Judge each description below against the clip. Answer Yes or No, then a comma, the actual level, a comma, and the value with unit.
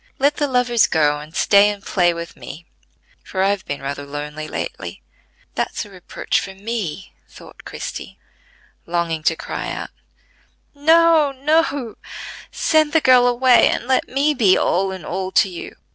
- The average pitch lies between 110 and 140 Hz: No, high, 200 Hz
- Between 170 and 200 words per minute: No, average, 160 wpm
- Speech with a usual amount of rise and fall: No, wide, 7.7 semitones